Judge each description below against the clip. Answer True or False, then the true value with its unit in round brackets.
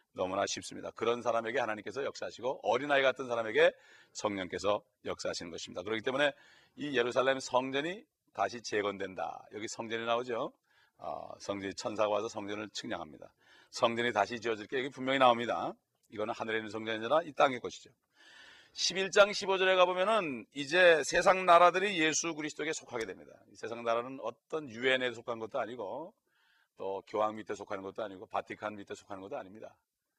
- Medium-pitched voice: False (120 Hz)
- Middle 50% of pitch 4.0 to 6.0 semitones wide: True (5.1 semitones)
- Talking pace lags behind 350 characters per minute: False (400 characters per minute)